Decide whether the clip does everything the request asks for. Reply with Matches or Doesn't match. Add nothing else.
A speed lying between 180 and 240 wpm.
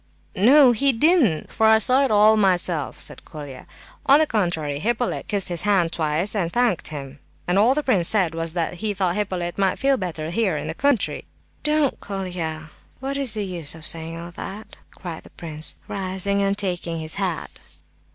Matches